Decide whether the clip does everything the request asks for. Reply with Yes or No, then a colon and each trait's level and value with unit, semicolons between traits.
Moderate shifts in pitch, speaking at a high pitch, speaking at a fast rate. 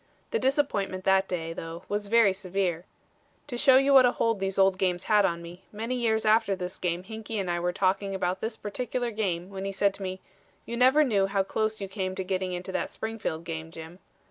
Yes: average, 3.2 semitones; high, 195 Hz; fast, 220 wpm